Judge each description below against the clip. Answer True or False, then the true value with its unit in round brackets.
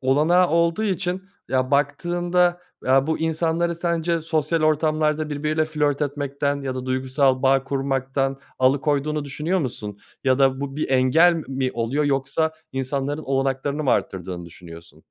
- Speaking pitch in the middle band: True (145 Hz)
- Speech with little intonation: False (3.1 semitones)